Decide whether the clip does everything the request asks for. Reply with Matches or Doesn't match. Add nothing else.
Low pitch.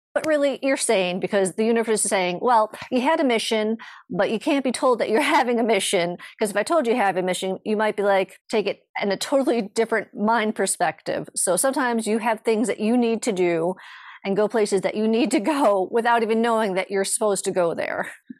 Doesn't match